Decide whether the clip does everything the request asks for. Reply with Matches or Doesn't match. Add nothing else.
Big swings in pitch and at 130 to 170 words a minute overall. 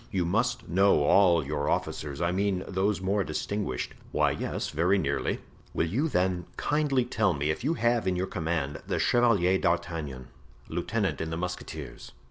Doesn't match